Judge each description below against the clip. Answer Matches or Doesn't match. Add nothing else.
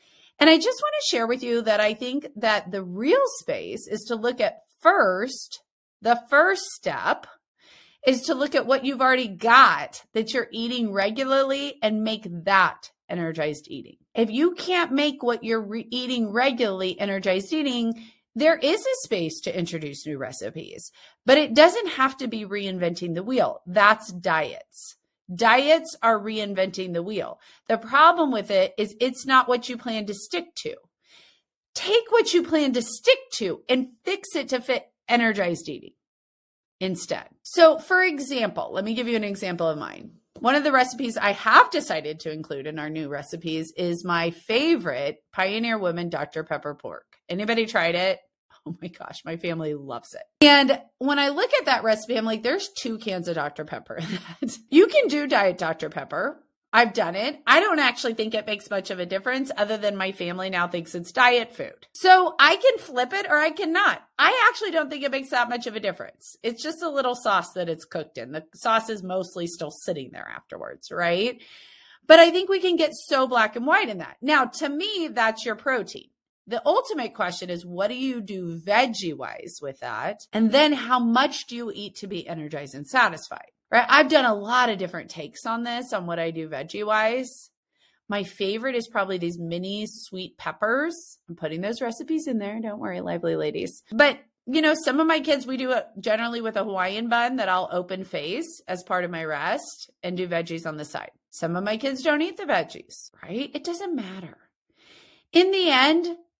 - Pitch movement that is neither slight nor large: Doesn't match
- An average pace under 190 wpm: Doesn't match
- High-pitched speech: Matches